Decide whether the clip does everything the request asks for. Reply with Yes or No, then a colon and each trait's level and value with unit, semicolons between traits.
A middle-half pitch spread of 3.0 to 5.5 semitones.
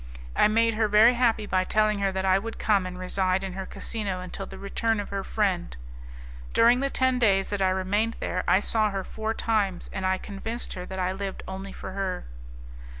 No: narrow, 2.6 semitones